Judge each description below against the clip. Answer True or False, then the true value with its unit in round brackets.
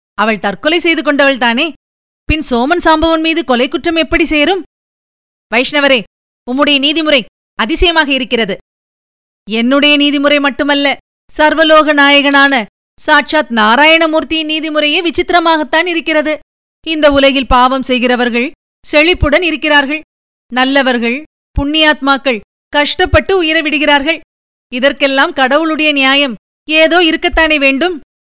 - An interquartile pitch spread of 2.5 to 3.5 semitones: True (2.8 semitones)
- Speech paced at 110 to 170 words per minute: False (95 wpm)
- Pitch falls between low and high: False (295 Hz)